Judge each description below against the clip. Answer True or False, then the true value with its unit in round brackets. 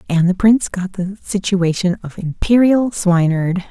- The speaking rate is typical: True (145 wpm)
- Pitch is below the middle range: False (190 Hz)